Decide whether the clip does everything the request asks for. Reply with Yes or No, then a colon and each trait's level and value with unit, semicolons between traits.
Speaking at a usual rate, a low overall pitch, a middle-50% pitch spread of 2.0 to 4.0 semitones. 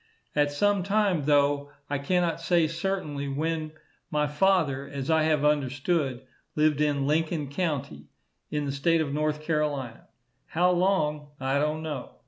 No: average, 145 wpm; medium, 150 Hz; narrow, 2.6 semitones